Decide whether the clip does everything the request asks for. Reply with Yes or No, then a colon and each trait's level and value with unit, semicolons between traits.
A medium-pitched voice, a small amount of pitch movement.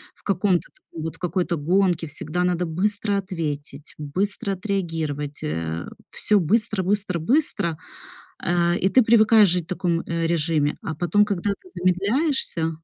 No: medium, 180 Hz; average, 3.7 semitones